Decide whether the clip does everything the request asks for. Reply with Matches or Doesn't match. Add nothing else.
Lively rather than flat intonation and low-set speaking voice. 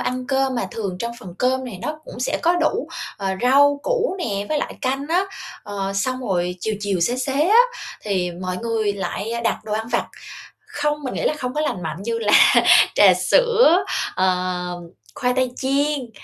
Doesn't match